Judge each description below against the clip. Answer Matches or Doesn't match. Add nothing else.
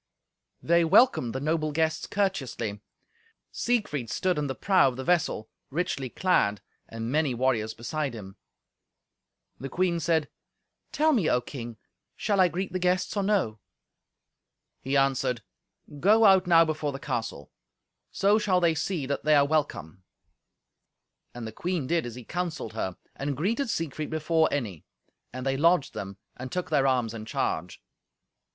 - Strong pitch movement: Matches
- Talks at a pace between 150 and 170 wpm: Matches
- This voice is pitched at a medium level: Matches